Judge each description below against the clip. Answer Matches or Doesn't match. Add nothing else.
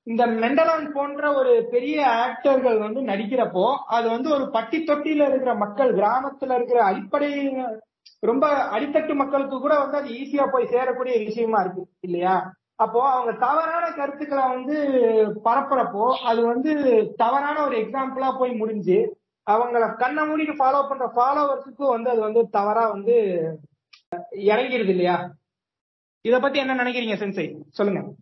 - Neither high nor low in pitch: Doesn't match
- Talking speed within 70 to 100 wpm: Doesn't match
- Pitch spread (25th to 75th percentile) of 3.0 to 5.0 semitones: Matches